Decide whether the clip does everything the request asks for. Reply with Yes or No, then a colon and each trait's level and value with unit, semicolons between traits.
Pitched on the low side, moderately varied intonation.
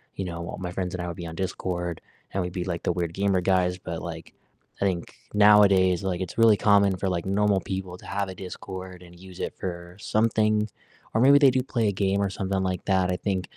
No: very low, 95 Hz; narrow, 2.1 semitones